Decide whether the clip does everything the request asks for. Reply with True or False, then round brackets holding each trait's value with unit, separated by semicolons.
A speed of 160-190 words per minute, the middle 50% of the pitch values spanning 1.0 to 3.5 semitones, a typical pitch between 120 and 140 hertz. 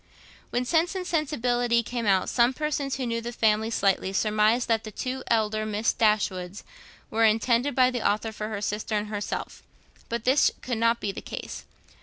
False (185 wpm; 2.7 semitones; 230 Hz)